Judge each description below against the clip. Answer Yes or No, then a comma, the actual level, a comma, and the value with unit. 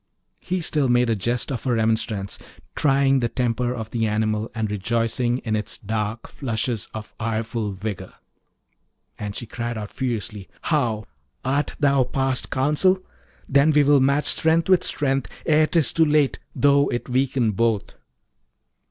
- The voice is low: Yes, low, 120 Hz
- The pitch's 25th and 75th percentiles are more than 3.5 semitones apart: Yes, average, 4.1 semitones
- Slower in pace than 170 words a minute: Yes, average, 150 wpm